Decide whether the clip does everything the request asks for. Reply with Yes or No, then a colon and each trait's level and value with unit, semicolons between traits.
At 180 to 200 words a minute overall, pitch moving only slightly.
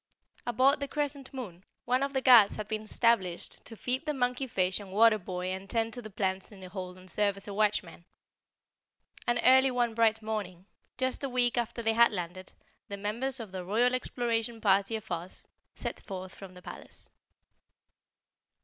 No: average, 185 wpm; average, 4.5 semitones